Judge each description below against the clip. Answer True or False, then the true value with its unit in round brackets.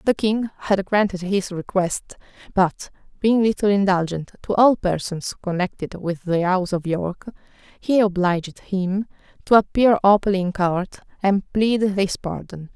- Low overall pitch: False (195 Hz)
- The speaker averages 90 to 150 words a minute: True (145 wpm)